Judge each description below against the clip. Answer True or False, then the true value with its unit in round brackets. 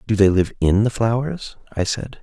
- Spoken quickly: True (215 wpm)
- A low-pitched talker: True (110 Hz)